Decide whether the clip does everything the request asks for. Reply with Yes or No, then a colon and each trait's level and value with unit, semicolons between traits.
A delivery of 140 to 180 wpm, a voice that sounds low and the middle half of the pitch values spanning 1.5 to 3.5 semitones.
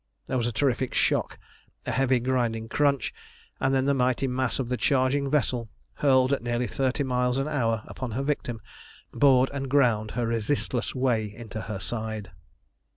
Yes: average, 170 wpm; low, 125 Hz; narrow, 2.6 semitones